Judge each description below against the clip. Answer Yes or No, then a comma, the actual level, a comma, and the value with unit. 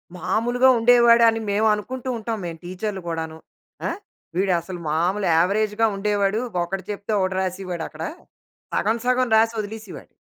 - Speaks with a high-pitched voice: Yes, high, 205 Hz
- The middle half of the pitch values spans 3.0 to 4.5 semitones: Yes, average, 3.6 semitones